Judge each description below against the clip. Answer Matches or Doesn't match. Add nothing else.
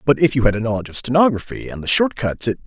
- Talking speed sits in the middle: Doesn't match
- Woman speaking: Doesn't match